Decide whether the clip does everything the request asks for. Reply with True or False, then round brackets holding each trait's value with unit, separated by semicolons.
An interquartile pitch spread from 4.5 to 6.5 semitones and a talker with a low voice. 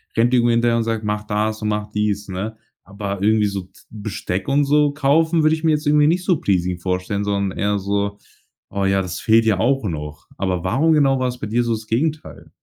True (5.2 semitones; 110 Hz)